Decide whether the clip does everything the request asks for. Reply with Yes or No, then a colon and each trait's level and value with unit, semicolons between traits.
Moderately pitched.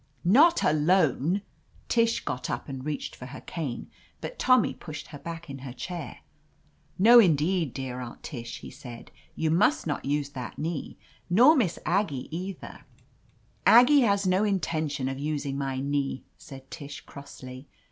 Yes: medium, 150 Hz